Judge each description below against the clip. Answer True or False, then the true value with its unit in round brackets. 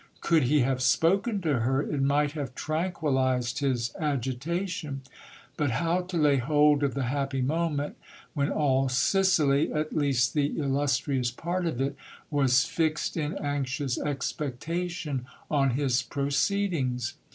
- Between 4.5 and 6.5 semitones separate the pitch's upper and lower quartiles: False (3.1 semitones)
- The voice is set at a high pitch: False (145 Hz)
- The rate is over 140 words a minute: False (135 wpm)